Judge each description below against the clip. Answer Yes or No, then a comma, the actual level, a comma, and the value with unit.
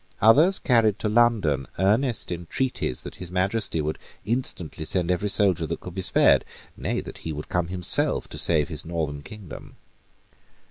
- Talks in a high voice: No, very low, 90 Hz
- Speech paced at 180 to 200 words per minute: No, average, 165 wpm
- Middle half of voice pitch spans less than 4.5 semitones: No, average, 5.1 semitones